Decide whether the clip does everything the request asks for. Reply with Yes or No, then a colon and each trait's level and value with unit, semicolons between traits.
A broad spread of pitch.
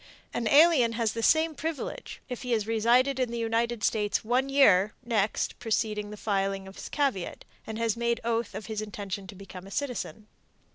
No: average, 3.0 semitones